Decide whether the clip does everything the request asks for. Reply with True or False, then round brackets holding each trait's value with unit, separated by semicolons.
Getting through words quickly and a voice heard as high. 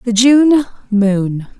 False (115 wpm; 230 Hz)